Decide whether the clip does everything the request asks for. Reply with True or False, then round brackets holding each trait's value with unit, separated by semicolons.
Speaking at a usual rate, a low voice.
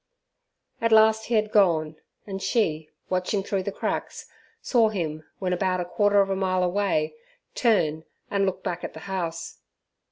False (165 wpm; 190 Hz)